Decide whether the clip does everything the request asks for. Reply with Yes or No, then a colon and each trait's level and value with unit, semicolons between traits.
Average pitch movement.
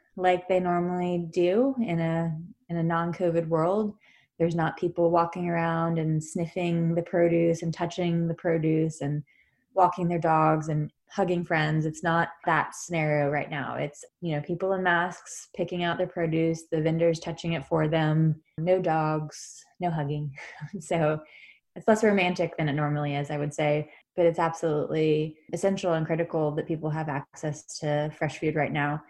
No: narrow, 2.0 semitones